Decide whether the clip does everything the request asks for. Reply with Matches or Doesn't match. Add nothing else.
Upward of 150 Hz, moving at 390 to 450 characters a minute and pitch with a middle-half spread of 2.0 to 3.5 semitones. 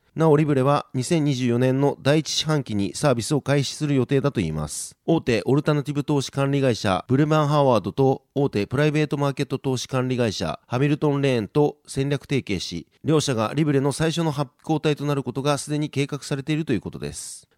Doesn't match